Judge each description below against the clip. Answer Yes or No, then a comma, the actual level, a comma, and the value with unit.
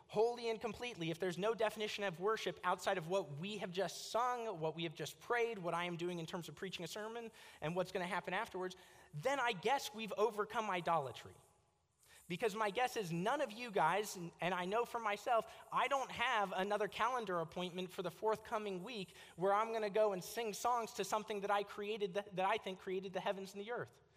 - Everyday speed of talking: No, fast, 225 wpm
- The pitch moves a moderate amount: Yes, average, 3.5 semitones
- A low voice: No, high, 200 Hz